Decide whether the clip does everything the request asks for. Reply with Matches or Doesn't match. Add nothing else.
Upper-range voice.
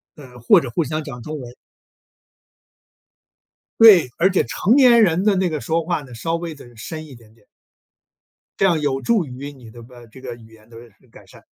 Doesn't match